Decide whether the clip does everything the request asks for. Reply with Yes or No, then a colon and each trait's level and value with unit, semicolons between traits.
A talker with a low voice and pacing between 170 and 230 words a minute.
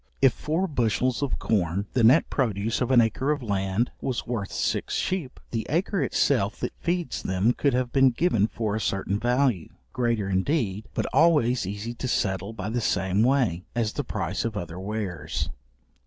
Yes: low, 115 Hz; average, 180 wpm